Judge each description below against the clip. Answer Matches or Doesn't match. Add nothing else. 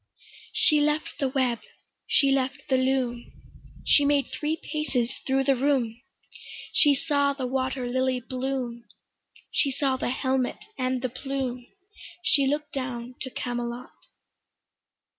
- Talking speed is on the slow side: Matches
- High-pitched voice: Matches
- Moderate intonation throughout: Doesn't match